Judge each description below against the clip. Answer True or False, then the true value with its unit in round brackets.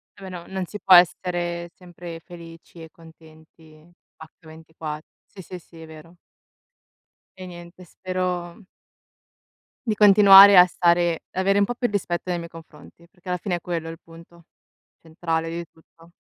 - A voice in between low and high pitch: True (175 Hz)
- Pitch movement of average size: False (1.9 semitones)